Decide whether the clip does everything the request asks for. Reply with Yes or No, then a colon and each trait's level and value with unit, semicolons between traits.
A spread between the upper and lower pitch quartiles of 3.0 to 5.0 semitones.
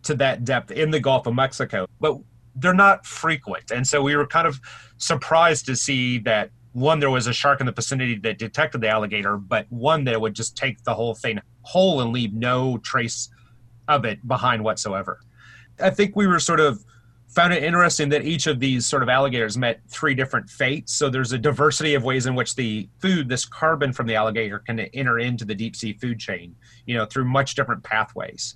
Yes: average, 4.1 semitones